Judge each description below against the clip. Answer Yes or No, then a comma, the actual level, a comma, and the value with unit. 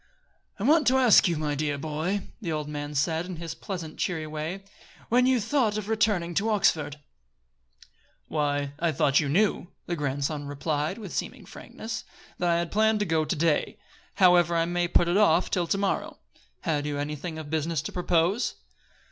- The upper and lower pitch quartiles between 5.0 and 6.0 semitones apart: No, average, 4.6 semitones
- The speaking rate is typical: Yes, average, 185 wpm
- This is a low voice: No, medium, 170 Hz